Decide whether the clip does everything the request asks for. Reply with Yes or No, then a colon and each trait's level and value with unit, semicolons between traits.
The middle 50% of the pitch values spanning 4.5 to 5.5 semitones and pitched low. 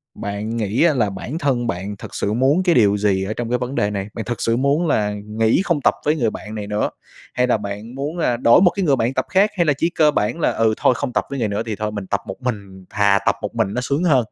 Yes: average, 5.1 semitones; low, 115 Hz